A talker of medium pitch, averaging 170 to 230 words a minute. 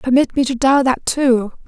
No: very high, 260 Hz; fast, 215 wpm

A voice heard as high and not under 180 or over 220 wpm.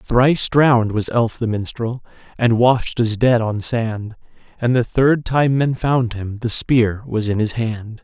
No: low, 115 Hz; average, 185 wpm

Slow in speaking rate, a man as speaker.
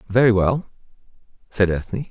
Yes: slow, 115 wpm; male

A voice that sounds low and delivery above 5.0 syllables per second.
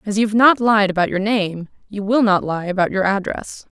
No: high, 205 Hz; 5.3 syllables/s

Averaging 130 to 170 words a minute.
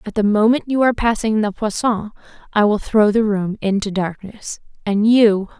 No: average, 180 wpm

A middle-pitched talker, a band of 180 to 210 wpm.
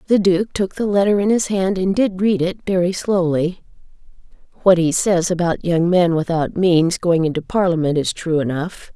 Yes: medium, 180 Hz; average, 190 wpm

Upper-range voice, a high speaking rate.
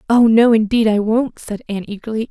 Yes: high, 220 Hz; fast, 210 wpm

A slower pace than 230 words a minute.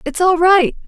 Yes: fast, 205 wpm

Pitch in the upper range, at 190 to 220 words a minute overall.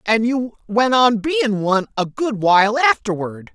No: high, 225 Hz; average, 170 wpm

